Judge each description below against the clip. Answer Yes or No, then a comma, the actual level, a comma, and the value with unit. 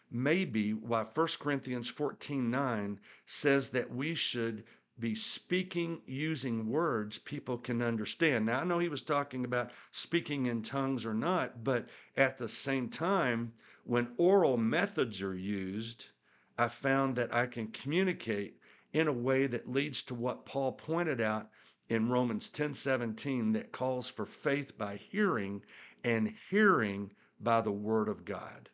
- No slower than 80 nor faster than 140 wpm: No, average, 150 wpm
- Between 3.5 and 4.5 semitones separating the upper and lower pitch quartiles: Yes, average, 4.2 semitones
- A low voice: Yes, low, 125 Hz